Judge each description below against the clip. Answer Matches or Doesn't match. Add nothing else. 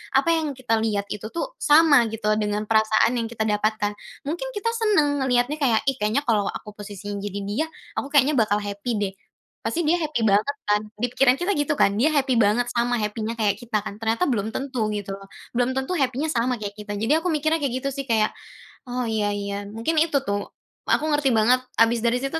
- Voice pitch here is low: Doesn't match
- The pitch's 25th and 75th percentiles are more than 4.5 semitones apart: Matches